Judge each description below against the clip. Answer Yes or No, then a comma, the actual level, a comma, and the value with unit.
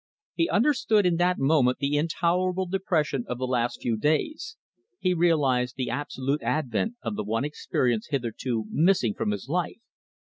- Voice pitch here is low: No, medium, 145 Hz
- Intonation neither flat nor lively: No, wide, 6.4 semitones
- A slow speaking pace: No, average, 155 wpm